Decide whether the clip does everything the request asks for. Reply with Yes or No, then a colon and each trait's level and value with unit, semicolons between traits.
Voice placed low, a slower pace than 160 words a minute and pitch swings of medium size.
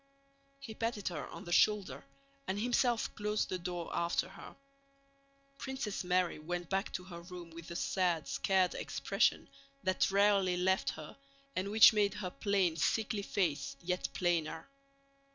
No: medium, 185 Hz; average, 150 wpm; average, 3.0 semitones